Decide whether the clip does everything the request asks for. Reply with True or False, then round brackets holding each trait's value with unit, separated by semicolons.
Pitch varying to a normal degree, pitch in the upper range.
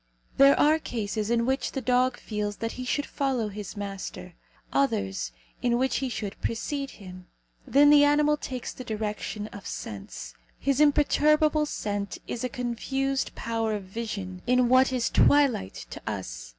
True (5.0 semitones; 235 Hz)